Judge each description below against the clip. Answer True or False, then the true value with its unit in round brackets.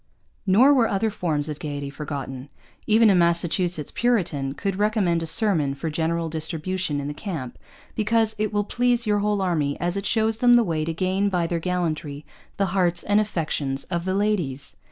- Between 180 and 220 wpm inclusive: True (185 wpm)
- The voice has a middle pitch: True (175 Hz)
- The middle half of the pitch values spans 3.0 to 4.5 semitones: False (5.2 semitones)